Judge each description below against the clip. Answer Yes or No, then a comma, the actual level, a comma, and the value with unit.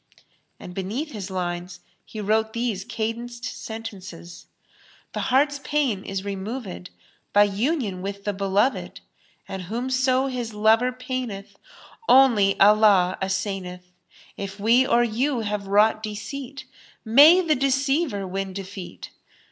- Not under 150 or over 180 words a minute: No, slow, 135 wpm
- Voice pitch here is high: Yes, high, 215 Hz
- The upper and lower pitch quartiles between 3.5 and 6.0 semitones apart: Yes, average, 4.5 semitones